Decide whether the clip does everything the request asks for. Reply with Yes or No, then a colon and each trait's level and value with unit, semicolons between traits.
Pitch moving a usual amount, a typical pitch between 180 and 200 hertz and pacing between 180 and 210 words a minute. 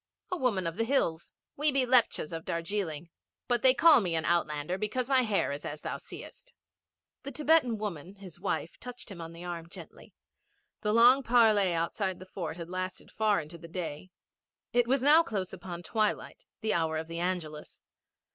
No: wide, 6.3 semitones; high, 190 Hz; average, 185 wpm